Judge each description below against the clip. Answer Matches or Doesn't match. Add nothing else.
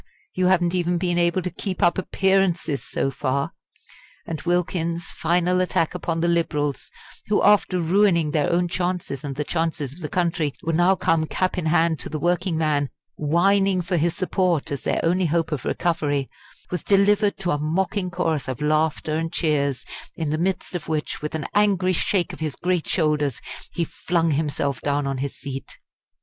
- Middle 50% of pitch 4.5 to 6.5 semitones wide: Doesn't match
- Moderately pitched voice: Matches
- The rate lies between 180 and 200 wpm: Matches